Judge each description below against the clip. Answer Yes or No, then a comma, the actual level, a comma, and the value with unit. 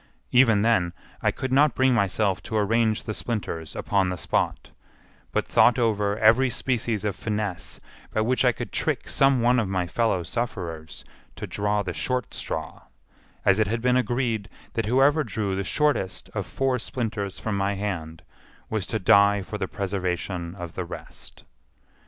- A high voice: No, low, 105 Hz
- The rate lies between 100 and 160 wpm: No, average, 170 wpm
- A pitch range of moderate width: Yes, average, 3.9 semitones